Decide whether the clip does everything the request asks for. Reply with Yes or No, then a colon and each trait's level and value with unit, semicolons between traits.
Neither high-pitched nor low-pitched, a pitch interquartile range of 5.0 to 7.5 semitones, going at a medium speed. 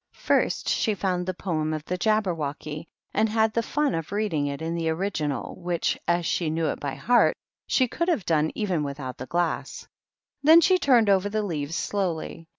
Yes: medium, 175 Hz; wide, 5.5 semitones; average, 190 wpm